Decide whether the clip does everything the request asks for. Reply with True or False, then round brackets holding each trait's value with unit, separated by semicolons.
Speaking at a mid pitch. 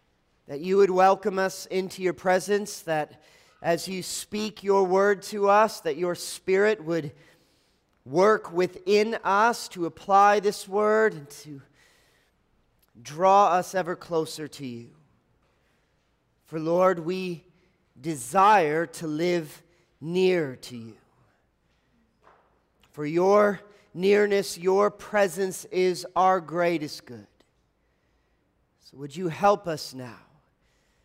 True (180 Hz)